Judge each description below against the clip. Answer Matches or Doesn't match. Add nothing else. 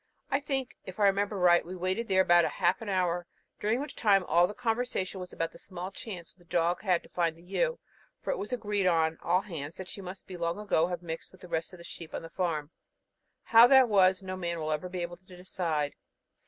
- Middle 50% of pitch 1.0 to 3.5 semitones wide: Matches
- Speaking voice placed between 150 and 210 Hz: Matches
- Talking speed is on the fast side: Matches